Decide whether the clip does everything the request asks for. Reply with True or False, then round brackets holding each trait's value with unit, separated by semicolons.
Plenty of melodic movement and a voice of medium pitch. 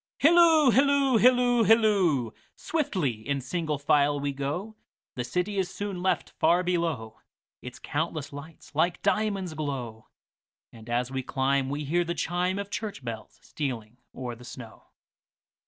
True (7.2 semitones; 160 Hz)